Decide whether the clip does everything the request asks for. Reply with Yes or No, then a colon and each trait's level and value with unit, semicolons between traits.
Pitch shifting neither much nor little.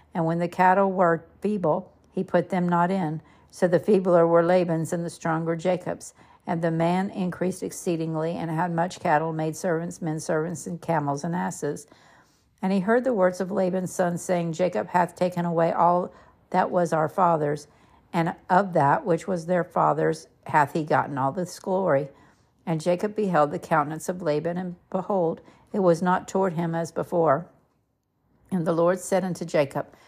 No: narrow, 2.0 semitones